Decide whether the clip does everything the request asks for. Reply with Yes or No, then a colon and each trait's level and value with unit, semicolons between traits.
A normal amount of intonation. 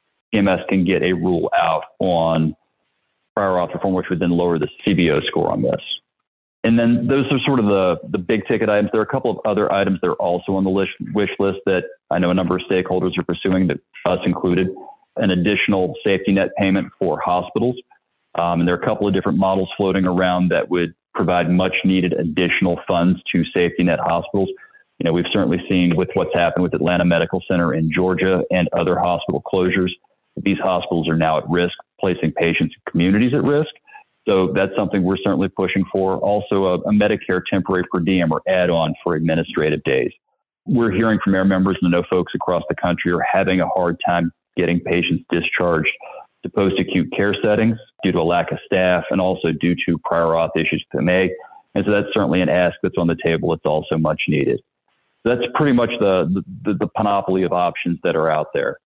No: narrow, 2.2 semitones